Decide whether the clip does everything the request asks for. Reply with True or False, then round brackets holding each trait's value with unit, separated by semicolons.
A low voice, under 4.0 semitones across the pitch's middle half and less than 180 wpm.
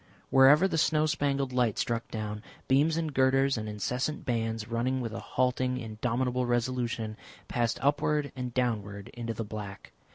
True (125 Hz; 3.0 semitones; 155 wpm)